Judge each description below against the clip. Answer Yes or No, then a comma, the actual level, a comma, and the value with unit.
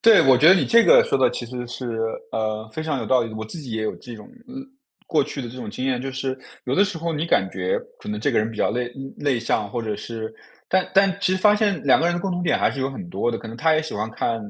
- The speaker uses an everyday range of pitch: No, wide, 7.0 semitones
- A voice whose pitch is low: Yes, low, 130 Hz